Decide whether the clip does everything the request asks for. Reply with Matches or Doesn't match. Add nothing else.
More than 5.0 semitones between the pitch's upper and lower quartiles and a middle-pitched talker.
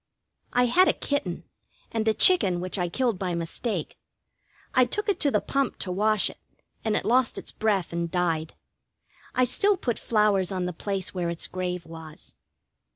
Doesn't match